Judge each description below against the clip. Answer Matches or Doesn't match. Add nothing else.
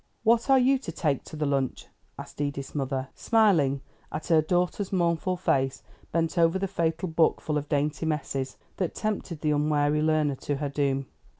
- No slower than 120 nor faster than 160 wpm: Doesn't match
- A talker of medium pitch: Matches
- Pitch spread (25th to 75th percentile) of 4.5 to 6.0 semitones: Doesn't match